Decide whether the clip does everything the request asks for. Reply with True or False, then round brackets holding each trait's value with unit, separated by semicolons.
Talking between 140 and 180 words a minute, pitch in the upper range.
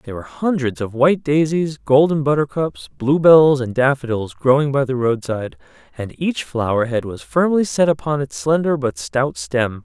False (170 wpm; 135 Hz)